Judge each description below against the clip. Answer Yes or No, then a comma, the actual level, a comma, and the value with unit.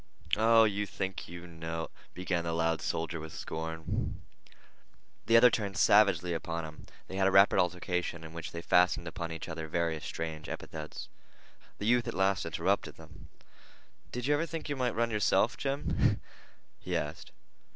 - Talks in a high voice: No, very low, 90 Hz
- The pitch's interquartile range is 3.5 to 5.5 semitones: Yes, average, 4.2 semitones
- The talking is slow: No, average, 165 wpm